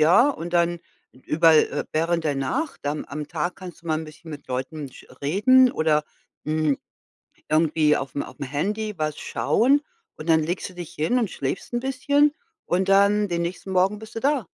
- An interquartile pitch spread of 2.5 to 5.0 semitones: No, wide, 5.4 semitones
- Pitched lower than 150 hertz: No, medium, 170 Hz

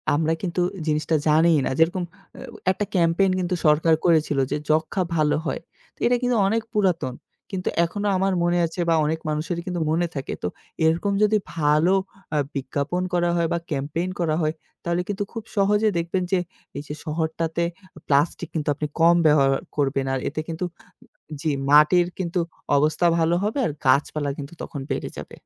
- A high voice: No, medium, 165 Hz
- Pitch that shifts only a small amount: No, average, 3.1 semitones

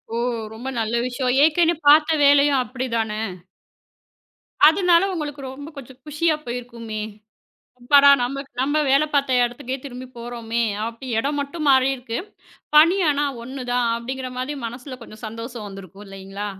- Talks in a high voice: Yes, very high, 255 Hz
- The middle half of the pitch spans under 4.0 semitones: Yes, average, 3.4 semitones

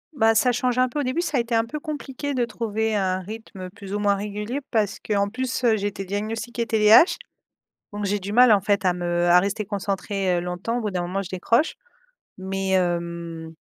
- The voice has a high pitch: Yes, high, 205 Hz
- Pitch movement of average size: Yes, average, 3.6 semitones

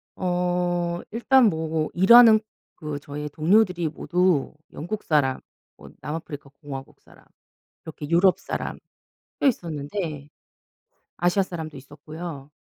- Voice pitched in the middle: Yes, medium, 165 Hz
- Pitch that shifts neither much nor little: Yes, average, 3.4 semitones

